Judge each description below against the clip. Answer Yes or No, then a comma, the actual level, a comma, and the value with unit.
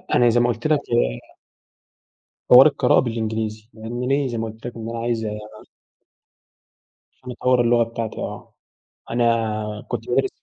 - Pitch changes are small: Yes, narrow, 1.6 semitones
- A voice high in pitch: No, low, 115 Hz